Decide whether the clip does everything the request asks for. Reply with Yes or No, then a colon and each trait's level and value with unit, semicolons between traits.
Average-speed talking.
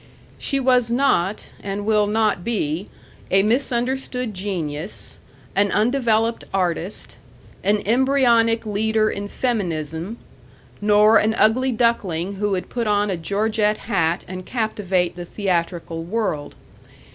No: slow, 120 wpm